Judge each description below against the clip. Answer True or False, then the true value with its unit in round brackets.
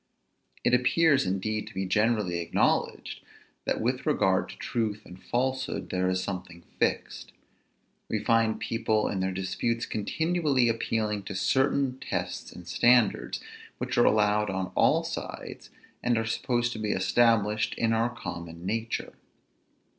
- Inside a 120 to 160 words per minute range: True (140 wpm)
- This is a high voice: False (110 Hz)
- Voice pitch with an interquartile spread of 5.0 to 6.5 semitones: False (4.0 semitones)